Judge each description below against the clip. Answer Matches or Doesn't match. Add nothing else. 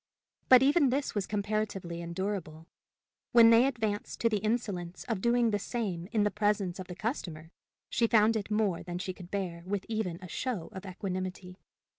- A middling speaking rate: Matches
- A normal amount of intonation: Matches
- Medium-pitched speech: Doesn't match